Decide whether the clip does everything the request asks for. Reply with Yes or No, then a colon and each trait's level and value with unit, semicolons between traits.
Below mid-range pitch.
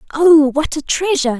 No: very high, 300 Hz